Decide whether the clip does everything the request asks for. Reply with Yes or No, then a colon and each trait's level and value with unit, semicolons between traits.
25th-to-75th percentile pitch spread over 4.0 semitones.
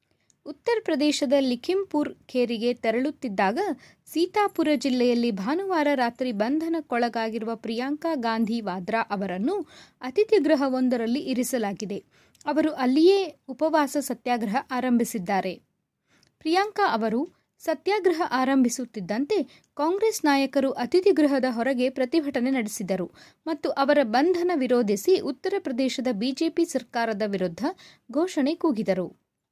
Yes: average, 5.0 semitones